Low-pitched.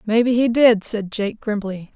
No: high, 220 Hz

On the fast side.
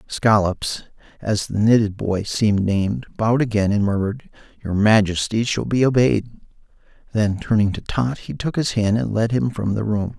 No: average, 175 wpm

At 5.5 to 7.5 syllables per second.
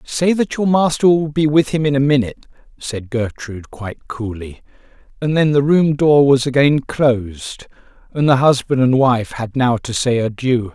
No: 4.8 syllables/s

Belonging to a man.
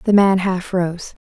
No: female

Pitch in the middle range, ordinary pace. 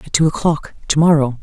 No: medium, 150 Hz; fast, 210 wpm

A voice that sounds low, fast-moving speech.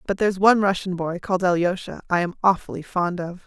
No: medium, 185 Hz; fast, 210 wpm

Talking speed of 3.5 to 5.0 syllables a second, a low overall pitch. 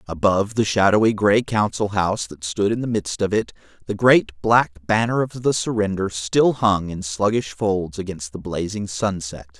Yes: 4.7 syllables/s; low, 100 Hz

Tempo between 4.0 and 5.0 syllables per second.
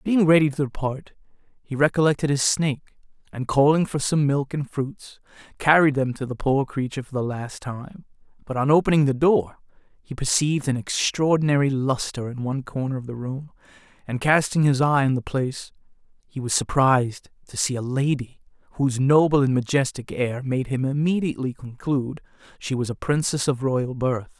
No: 5.4 syllables/s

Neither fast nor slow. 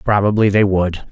Yes: average, 160 wpm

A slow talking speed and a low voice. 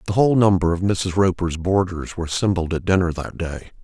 No: fast, 205 wpm; very low, 90 Hz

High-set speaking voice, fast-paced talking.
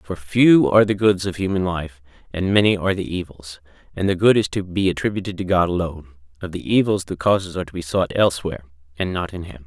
No: very low, 90 Hz; fast, 230 wpm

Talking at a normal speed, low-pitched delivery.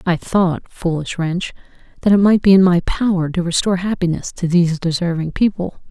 No: average, 185 wpm; medium, 180 Hz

